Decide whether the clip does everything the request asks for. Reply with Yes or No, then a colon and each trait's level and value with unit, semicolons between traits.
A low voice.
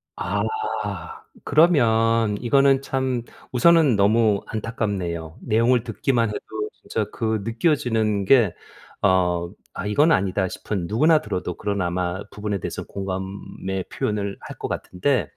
Yes: low, 105 Hz